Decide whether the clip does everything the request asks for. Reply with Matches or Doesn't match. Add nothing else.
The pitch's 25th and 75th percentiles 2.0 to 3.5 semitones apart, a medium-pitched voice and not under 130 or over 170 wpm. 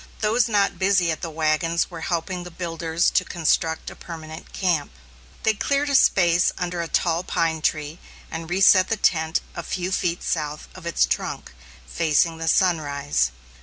Matches